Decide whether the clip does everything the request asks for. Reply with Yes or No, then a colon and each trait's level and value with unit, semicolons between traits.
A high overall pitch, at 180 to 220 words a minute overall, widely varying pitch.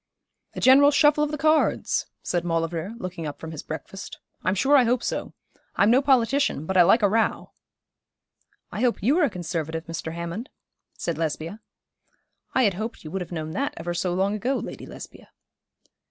Yes: high, 195 Hz; average, 185 wpm; wide, 7.5 semitones